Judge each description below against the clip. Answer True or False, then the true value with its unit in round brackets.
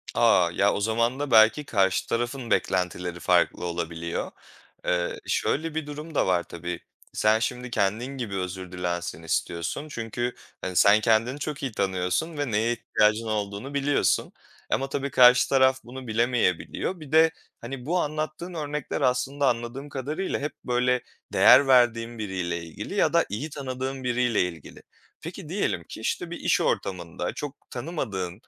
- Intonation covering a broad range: True (6.2 semitones)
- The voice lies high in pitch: False (120 Hz)